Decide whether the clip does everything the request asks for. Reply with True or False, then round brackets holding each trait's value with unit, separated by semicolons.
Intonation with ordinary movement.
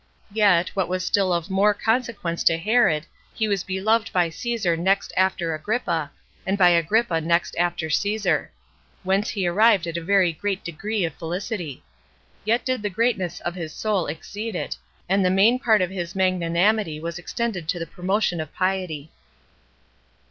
True (3.6 semitones)